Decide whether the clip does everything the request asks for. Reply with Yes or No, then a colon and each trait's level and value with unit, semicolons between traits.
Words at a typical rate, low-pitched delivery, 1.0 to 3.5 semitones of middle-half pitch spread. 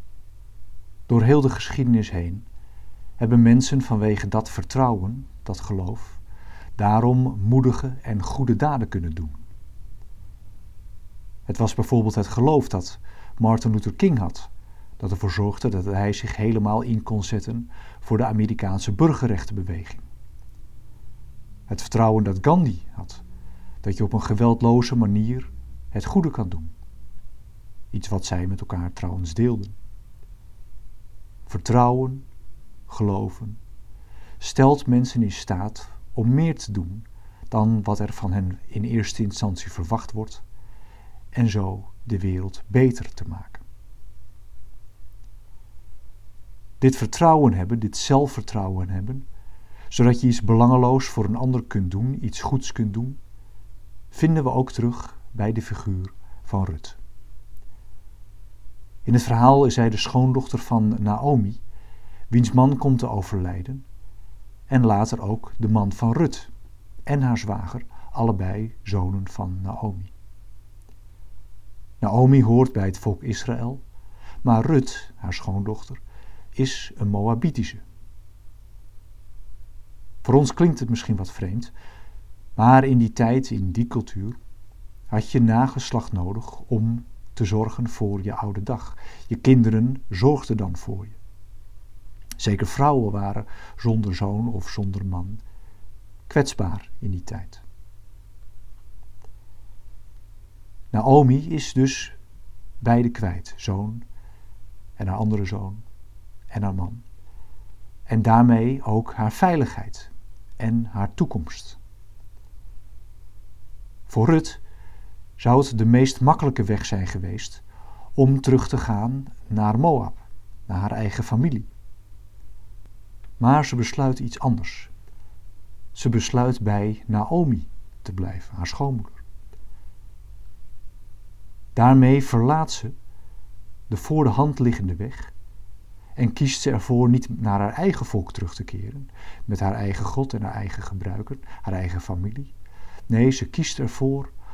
No: slow, 120 wpm; low, 105 Hz; average, 2.9 semitones